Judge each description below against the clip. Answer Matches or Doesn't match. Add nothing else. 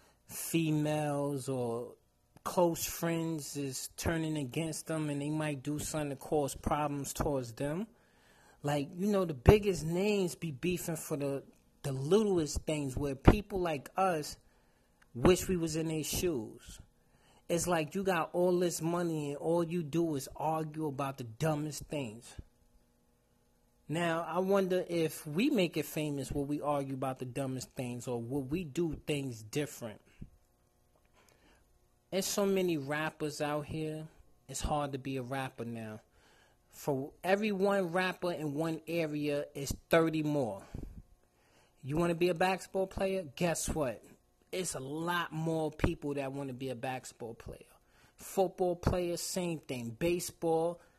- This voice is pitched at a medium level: Matches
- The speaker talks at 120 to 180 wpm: Matches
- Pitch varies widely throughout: Doesn't match